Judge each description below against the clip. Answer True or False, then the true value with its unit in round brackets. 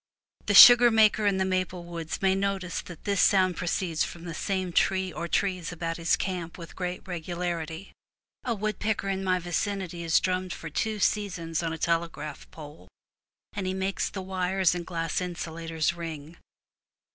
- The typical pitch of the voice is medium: True (180 Hz)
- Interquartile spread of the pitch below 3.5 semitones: True (2.4 semitones)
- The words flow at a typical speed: True (170 wpm)